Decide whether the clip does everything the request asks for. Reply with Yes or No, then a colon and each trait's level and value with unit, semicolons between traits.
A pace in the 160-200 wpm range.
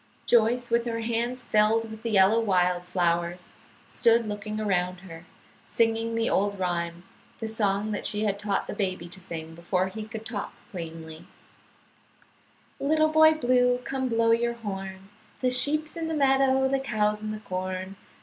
Yes: average, 165 wpm